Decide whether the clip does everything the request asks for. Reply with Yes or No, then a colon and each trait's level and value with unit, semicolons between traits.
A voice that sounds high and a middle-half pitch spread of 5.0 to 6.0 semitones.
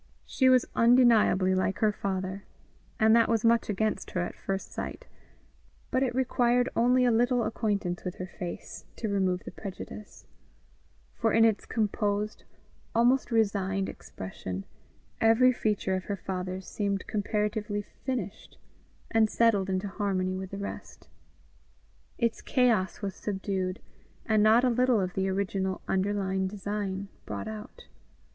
No: high, 205 Hz; average, 3.1 semitones